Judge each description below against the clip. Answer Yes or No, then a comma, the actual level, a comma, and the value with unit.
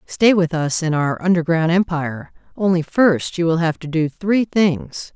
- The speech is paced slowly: No, average, 185 wpm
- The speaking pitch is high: No, medium, 170 Hz